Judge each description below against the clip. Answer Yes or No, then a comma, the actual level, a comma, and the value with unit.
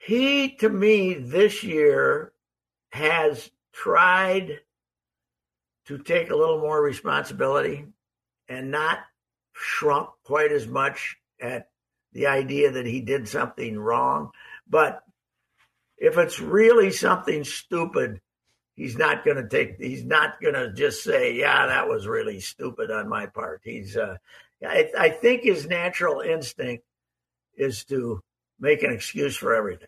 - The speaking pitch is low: No, high, 190 Hz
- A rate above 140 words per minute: No, slow, 135 wpm